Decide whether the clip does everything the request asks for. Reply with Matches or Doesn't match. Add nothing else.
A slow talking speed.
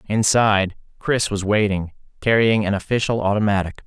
Matches